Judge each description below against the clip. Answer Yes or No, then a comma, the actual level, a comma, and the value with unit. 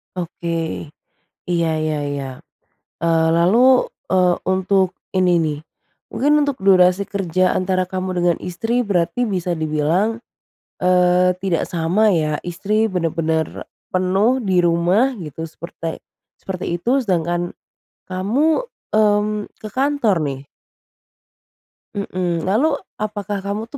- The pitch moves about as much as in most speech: Yes, average, 3.7 semitones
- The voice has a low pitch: No, medium, 185 Hz